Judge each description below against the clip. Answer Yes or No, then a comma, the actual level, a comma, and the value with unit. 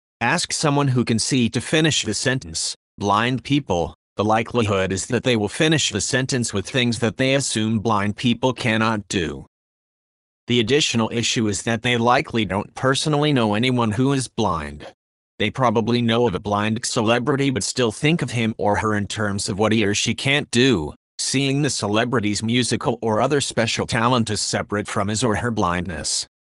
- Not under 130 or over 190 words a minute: Yes, average, 185 wpm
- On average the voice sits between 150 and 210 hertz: No, low, 115 Hz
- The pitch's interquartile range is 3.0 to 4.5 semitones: Yes, average, 3.5 semitones